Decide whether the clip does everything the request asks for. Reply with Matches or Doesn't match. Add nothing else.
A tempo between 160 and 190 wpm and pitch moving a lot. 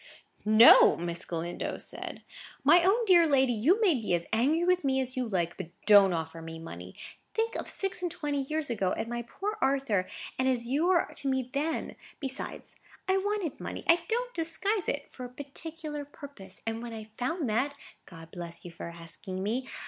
Matches